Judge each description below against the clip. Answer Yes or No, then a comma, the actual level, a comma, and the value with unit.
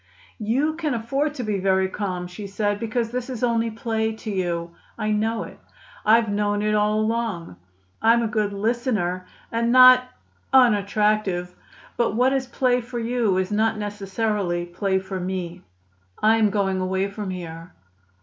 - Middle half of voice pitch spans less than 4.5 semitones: Yes, average, 3.6 semitones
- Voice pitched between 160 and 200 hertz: No, high, 215 Hz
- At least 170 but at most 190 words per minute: No, average, 160 wpm